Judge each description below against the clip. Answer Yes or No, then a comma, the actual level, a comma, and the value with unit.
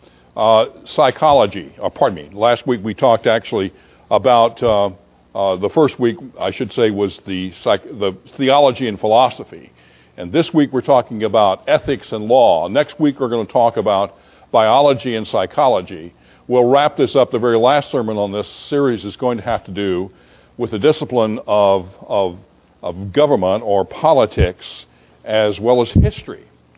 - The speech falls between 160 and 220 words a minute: Yes, average, 170 wpm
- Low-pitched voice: Yes, low, 110 Hz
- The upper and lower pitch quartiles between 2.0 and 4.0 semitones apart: No, average, 4.8 semitones